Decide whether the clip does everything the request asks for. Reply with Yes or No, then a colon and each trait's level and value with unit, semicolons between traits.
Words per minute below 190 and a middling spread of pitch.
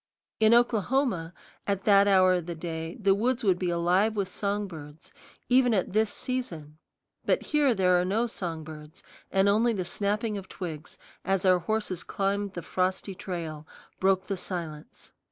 Yes: average, 170 wpm; average, 3.4 semitones